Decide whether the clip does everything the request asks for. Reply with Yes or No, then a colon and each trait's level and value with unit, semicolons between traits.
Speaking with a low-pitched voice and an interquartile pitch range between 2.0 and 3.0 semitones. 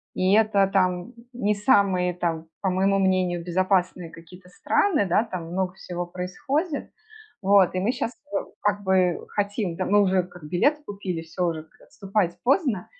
No: high, 190 Hz; narrow, 2.5 semitones